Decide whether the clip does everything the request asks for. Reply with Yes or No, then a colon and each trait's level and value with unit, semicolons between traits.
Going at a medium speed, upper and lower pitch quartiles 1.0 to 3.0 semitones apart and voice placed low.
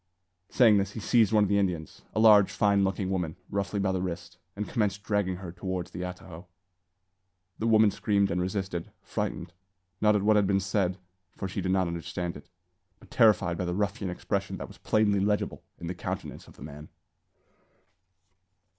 Yes: average, 185 wpm; narrow, 2.4 semitones; very low, 95 Hz